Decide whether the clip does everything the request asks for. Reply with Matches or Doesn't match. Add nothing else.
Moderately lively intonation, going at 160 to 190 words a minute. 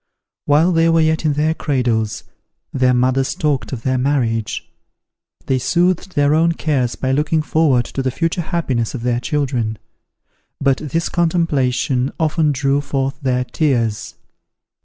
Doesn't match